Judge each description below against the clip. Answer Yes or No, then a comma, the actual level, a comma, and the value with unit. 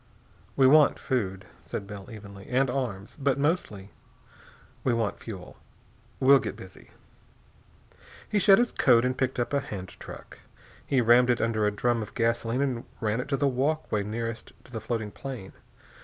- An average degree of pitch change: Yes, average, 4.1 semitones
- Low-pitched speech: Yes, low, 120 Hz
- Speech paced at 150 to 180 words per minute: Yes, average, 170 wpm